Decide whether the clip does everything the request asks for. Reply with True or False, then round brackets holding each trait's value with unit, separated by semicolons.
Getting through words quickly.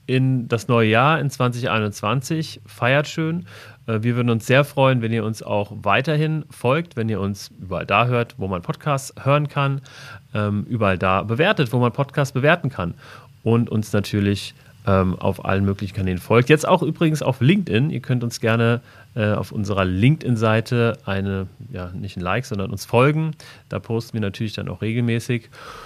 False (170 wpm)